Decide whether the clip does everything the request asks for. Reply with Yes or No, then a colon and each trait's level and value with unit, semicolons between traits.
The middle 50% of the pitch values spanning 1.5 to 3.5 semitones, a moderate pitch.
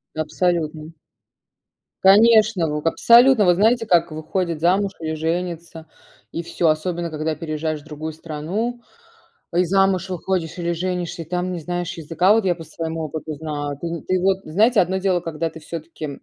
Yes: average, 2.8 semitones; medium, 170 Hz